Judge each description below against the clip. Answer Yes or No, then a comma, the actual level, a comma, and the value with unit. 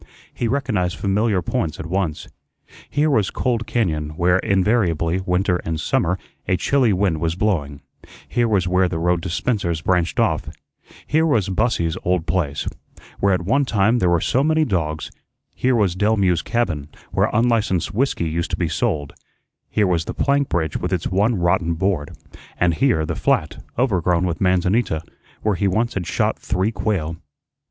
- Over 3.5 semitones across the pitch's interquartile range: Yes, average, 4.6 semitones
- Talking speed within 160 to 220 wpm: Yes, average, 170 wpm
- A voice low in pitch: Yes, very low, 95 Hz